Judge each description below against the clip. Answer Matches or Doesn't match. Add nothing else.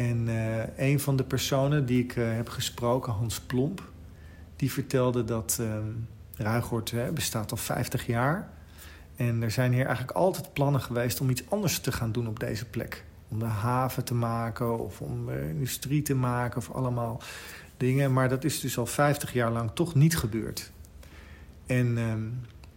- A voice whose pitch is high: Doesn't match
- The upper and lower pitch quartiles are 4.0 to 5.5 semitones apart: Doesn't match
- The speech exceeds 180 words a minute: Doesn't match